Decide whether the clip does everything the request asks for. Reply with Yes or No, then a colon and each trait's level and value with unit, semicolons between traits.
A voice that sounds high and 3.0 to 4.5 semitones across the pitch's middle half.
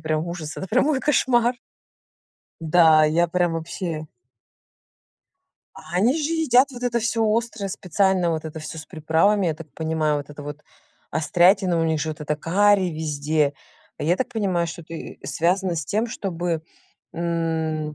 No: medium, 170 Hz; average, 4.1 semitones